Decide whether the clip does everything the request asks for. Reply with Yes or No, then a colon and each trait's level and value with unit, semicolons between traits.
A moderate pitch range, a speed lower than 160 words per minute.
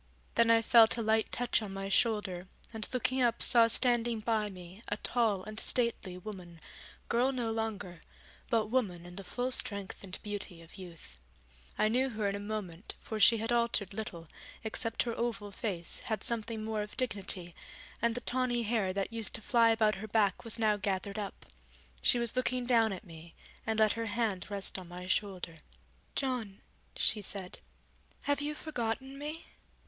No: average, 3.1 semitones; average, 180 wpm